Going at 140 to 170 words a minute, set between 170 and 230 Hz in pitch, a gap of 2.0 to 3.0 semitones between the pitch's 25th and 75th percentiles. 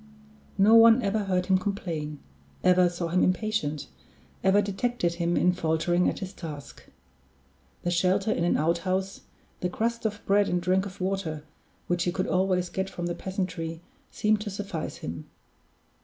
Yes: average, 160 wpm; medium, 185 Hz; narrow, 2.5 semitones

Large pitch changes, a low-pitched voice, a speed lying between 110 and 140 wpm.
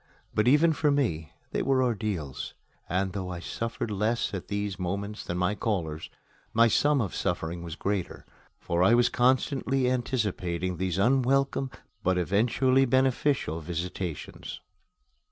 Yes: wide, 6.1 semitones; low, 105 Hz; slow, 135 wpm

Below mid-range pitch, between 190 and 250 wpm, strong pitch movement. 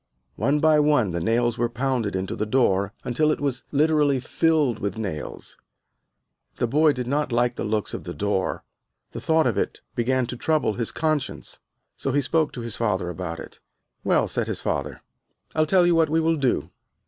Yes: low, 125 Hz; average, 195 wpm; wide, 5.7 semitones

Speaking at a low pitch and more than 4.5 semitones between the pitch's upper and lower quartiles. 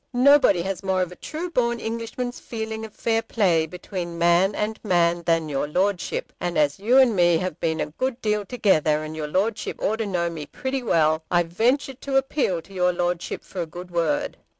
No: medium, 185 Hz; average, 5.1 semitones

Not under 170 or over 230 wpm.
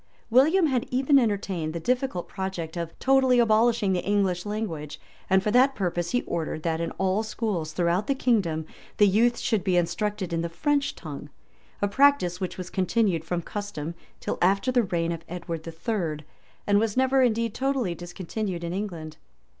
Yes: average, 180 wpm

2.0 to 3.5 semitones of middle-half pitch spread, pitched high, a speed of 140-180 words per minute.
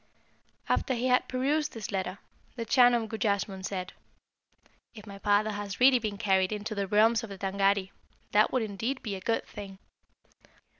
Yes: average, 2.9 semitones; high, 210 Hz; average, 170 wpm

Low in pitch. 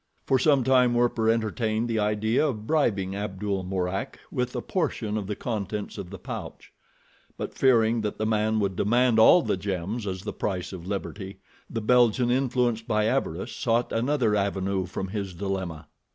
Yes: low, 110 Hz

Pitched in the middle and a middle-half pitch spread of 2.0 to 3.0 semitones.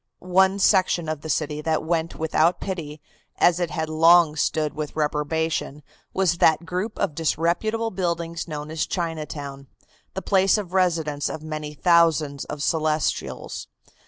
Yes: medium, 160 Hz; narrow, 2.5 semitones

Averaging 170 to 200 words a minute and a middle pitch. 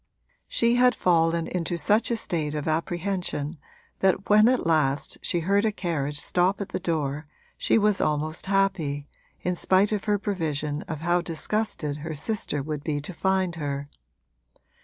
No: average, 160 wpm; medium, 170 Hz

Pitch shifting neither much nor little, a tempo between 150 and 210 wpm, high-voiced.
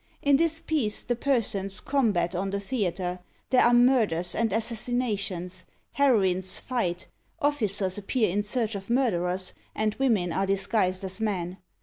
No: average, 4.6 semitones; average, 140 wpm; high, 205 Hz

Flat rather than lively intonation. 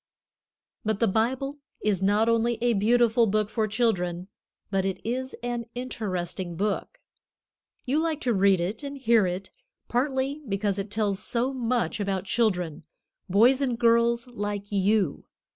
No: average, 3.7 semitones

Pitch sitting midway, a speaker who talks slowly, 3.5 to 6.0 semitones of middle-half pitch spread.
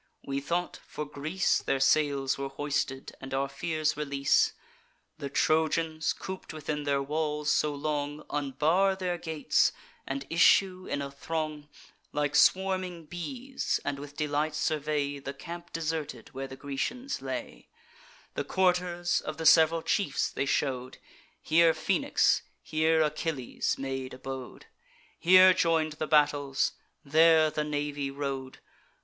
No: medium, 150 Hz; slow, 130 wpm; average, 2.9 semitones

